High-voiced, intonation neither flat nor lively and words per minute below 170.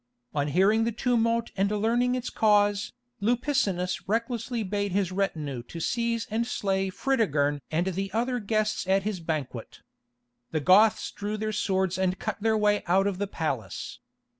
Yes: high, 205 Hz; average, 3.6 semitones; average, 155 wpm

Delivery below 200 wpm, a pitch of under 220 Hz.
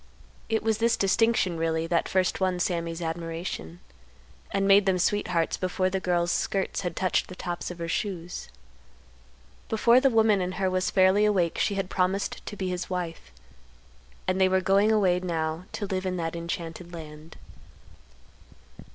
Yes: average, 165 wpm; medium, 185 Hz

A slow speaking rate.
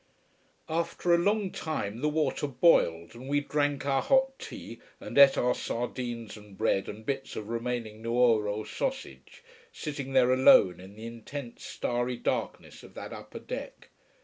No: average, 155 wpm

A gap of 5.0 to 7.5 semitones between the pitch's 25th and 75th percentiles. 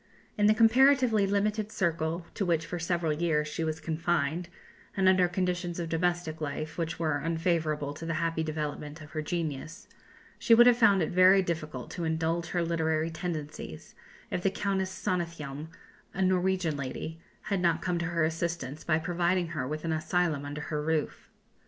No: narrow, 2.5 semitones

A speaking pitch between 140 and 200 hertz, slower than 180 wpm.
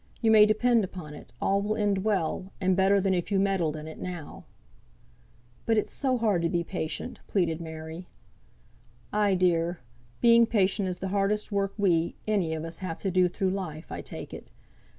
No: high, 190 Hz; average, 190 wpm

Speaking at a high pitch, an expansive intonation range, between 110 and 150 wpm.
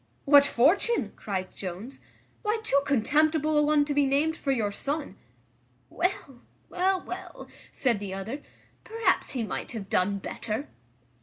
Yes: very high, 280 Hz; wide, 6.3 semitones; average, 145 wpm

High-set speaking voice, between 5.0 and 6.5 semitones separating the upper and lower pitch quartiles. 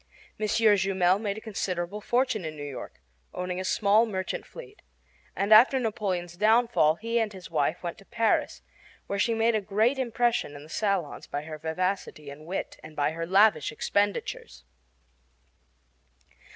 No: high, 195 Hz; average, 4.5 semitones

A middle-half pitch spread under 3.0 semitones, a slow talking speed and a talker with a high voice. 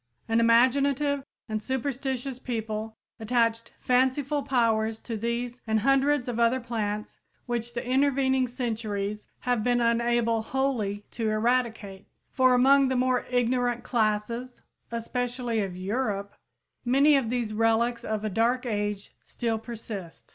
Yes: narrow, 2.5 semitones; slow, 130 wpm; high, 235 Hz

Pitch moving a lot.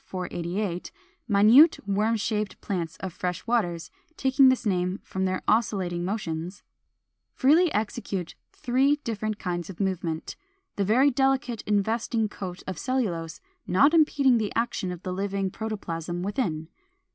No: average, 4.6 semitones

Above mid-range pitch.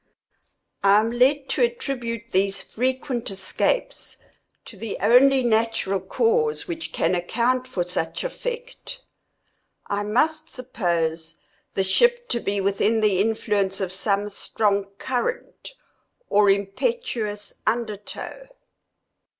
Yes: high, 225 Hz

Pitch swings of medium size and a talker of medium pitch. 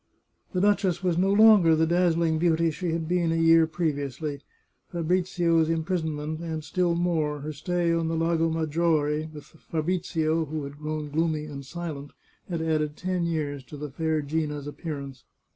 No: narrow, 2.0 semitones; medium, 160 Hz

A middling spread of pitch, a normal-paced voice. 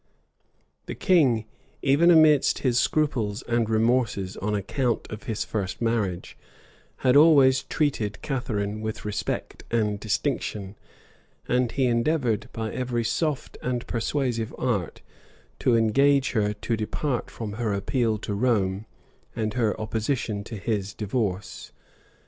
No: average, 3.5 semitones; slow, 130 wpm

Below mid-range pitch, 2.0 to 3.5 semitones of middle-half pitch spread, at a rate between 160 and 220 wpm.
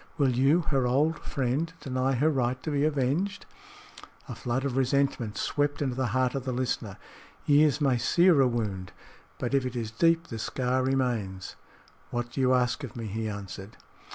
Yes: low, 130 Hz; average, 3.0 semitones; average, 180 wpm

